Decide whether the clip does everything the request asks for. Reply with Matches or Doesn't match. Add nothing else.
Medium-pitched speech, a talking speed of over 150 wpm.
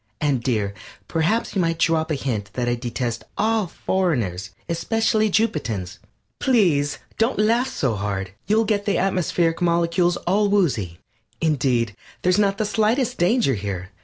Doesn't match